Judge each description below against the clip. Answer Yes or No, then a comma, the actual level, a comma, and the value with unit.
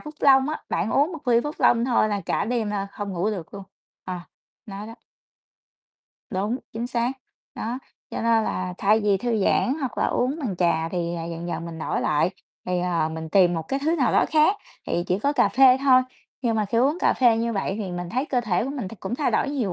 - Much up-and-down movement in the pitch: Yes, wide, 5.9 semitones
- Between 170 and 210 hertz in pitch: No, high, 220 Hz